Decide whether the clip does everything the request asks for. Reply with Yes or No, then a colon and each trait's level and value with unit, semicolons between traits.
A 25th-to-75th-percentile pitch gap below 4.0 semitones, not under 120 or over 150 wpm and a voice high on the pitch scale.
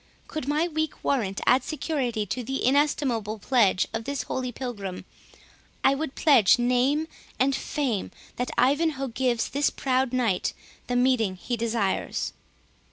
Yes: average, 3.5 semitones; average, 140 wpm; very high, 255 Hz